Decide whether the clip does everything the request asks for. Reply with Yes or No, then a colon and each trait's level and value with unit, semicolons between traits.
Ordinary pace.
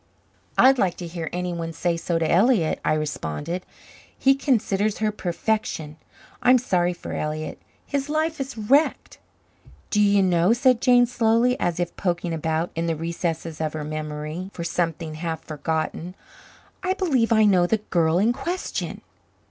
Yes: average, 160 wpm